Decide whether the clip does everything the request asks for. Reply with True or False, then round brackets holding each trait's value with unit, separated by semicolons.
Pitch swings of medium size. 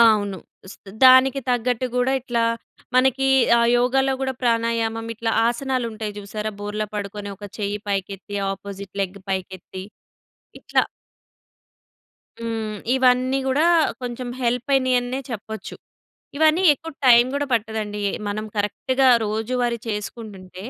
True (3.6 semitones)